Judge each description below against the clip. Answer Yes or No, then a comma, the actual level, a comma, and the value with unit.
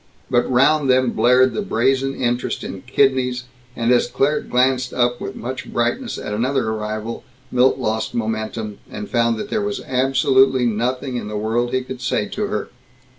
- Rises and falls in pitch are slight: Yes, narrow, 2.1 semitones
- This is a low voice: Yes, low, 125 Hz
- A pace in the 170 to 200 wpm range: Yes, average, 175 wpm